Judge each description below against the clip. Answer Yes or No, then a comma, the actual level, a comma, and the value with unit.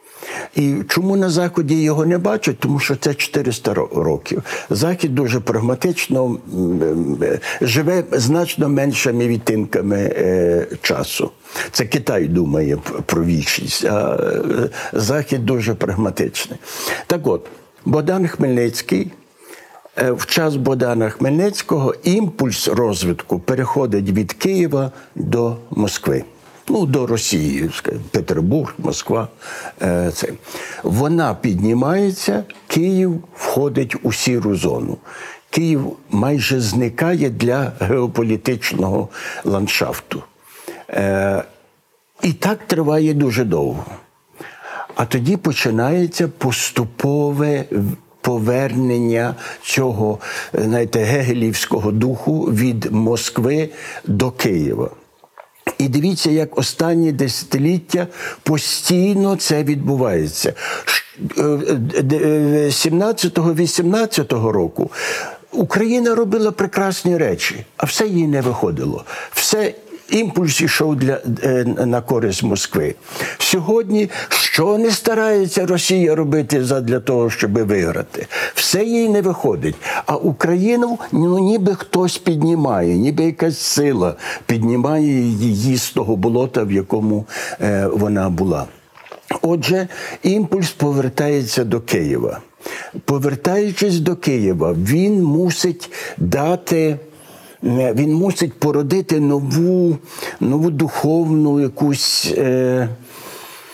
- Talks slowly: Yes, slow, 90 wpm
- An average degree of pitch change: No, wide, 6.2 semitones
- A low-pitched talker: No, medium, 145 Hz